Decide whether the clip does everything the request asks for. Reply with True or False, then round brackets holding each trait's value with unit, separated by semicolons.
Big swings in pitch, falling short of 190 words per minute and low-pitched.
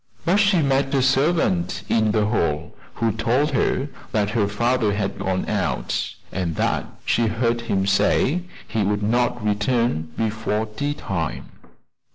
False (4.0 semitones; 150 wpm; 110 Hz)